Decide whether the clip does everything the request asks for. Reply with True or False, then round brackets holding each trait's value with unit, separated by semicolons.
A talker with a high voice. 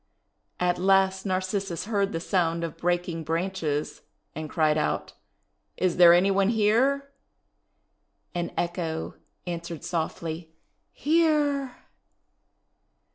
False (180 Hz)